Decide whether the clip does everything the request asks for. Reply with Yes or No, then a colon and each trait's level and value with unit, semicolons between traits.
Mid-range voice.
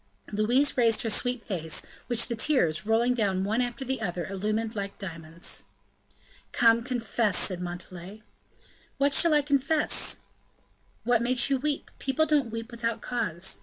No: high, 230 Hz